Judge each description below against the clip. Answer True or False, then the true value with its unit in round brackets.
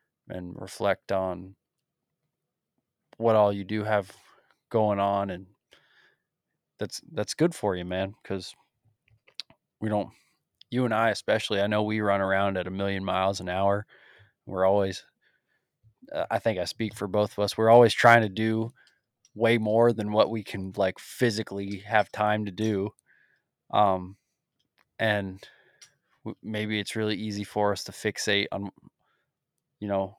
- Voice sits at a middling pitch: False (105 Hz)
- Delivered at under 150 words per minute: False (155 wpm)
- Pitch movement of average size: False (2.2 semitones)